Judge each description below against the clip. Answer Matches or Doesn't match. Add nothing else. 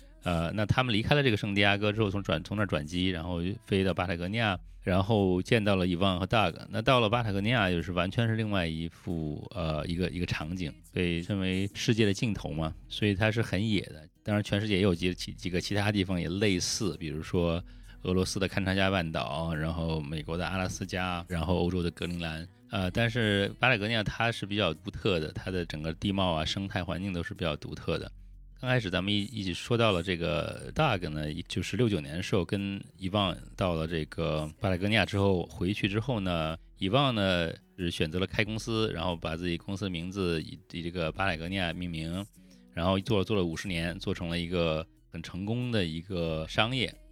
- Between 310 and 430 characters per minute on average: Matches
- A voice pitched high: Doesn't match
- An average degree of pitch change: Matches